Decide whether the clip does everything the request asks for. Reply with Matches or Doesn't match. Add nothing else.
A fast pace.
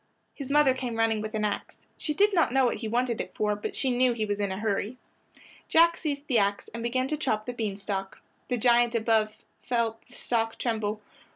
Matches